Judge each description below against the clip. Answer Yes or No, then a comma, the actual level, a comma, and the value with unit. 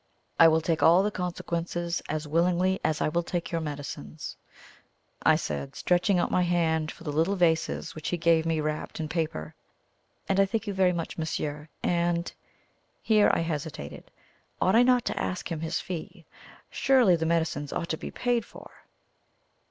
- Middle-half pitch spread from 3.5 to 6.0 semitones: No, narrow, 2.4 semitones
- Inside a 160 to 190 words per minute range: Yes, average, 175 wpm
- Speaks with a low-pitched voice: No, medium, 170 Hz